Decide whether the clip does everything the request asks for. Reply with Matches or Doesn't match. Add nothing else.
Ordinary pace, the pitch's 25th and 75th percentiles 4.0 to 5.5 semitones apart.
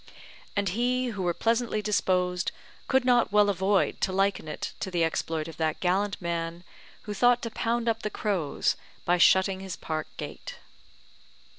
Matches